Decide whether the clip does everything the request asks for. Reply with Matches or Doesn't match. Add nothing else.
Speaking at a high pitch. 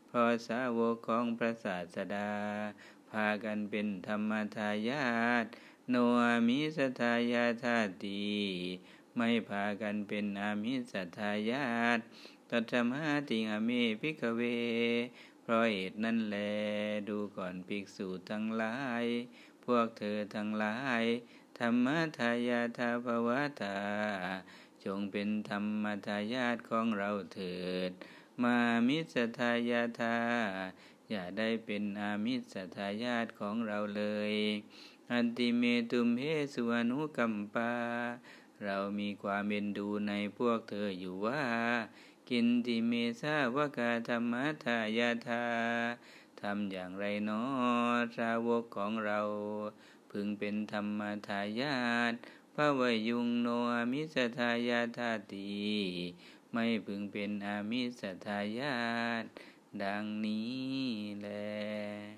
Doesn't match